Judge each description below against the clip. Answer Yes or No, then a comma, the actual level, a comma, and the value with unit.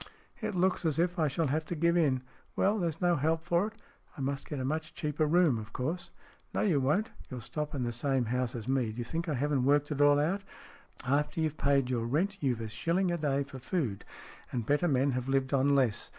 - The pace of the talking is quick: Yes, fast, 235 wpm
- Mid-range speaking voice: Yes, medium, 145 Hz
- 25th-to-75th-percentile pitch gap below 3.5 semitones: No, average, 4.3 semitones